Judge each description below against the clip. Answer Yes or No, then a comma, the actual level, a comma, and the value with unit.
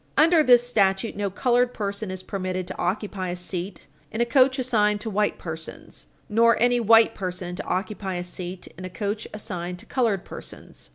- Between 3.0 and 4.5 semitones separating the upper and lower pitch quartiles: Yes, average, 4.0 semitones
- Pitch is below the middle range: No, high, 205 Hz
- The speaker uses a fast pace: No, average, 185 wpm